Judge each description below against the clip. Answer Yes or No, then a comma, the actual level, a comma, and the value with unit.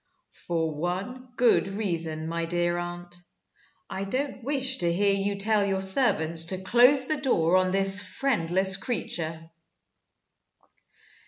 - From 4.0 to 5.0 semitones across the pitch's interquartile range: Yes, average, 4.5 semitones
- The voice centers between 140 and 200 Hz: Yes, high, 190 Hz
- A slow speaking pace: Yes, slow, 130 wpm